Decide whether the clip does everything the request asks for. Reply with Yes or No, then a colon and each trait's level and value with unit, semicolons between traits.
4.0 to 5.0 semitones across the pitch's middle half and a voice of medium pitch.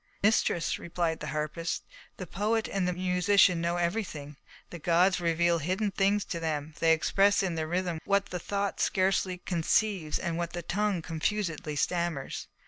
No: average, 3.0 semitones; medium, 175 Hz